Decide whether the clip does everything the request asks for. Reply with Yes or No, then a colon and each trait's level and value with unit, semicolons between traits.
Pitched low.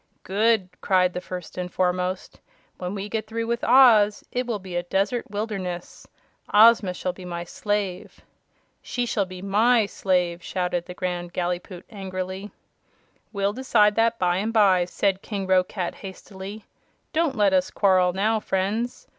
No: high, 195 Hz